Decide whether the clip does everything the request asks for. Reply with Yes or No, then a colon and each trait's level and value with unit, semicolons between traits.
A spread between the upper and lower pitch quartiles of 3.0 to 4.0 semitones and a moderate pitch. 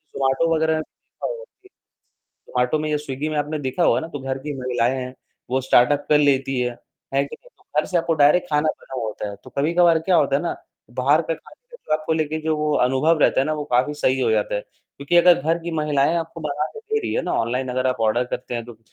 Yes: average, 3.6 semitones; medium, 145 Hz